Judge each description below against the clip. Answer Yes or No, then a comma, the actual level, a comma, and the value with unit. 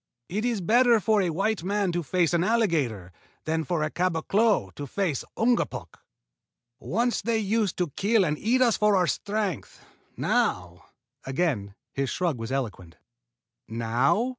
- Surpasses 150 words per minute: Yes, average, 160 wpm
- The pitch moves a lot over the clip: Yes, wide, 7.8 semitones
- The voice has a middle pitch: Yes, medium, 180 Hz